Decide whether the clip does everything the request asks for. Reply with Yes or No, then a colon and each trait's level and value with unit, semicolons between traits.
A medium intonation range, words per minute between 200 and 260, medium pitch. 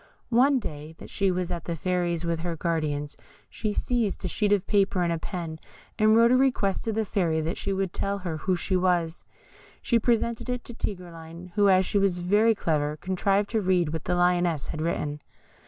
Yes: average, 3.7 semitones; fast, 205 wpm; medium, 180 Hz